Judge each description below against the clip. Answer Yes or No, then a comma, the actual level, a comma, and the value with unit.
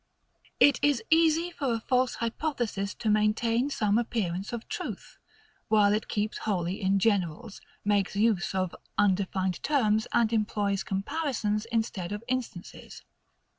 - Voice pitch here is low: No, high, 215 Hz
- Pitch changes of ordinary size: Yes, average, 3.2 semitones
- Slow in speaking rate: Yes, slow, 130 wpm